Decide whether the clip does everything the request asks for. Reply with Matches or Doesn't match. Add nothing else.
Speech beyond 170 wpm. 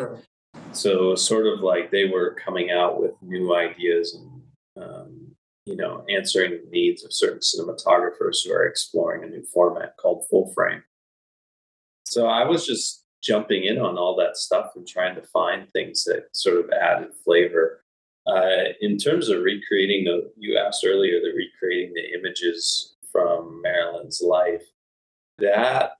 Doesn't match